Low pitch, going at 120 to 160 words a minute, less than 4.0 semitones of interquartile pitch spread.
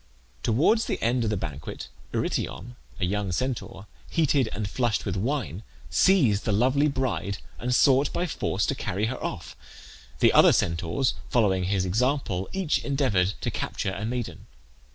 No: low, 115 Hz; average, 155 wpm; wide, 5.5 semitones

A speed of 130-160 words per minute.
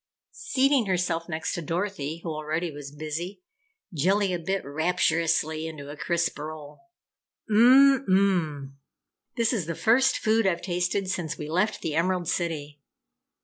Yes: average, 140 wpm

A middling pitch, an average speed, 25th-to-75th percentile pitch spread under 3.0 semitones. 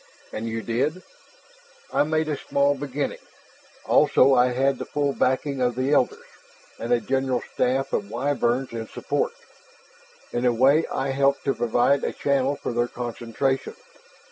No: low, 130 Hz; average, 155 wpm; narrow, 2.6 semitones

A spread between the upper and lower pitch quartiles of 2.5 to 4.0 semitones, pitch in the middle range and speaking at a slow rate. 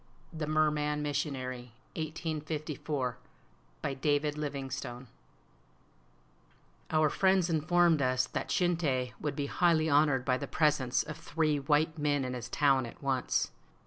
Yes: average, 2.9 semitones; medium, 150 Hz; slow, 125 wpm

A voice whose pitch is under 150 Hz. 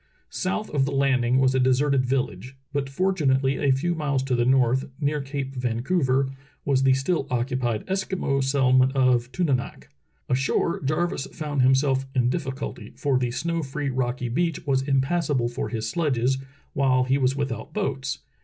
Yes: low, 135 Hz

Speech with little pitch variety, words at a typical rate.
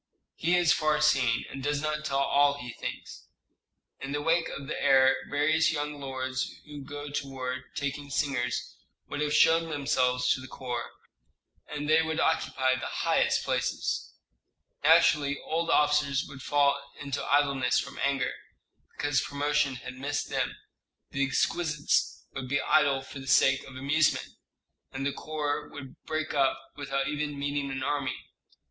Yes: narrow, 1.8 semitones; average, 155 wpm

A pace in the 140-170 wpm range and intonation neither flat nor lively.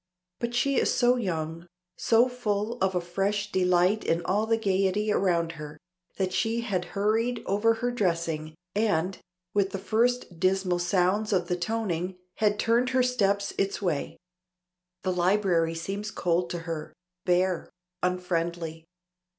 Yes: average, 145 wpm; average, 3.7 semitones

